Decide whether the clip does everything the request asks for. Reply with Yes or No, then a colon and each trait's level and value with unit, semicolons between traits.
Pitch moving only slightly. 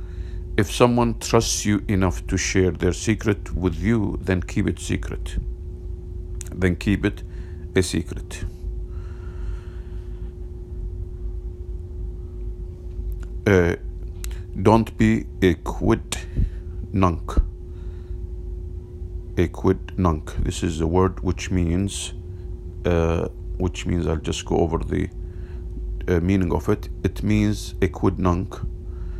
Yes: narrow, 1.0 semitones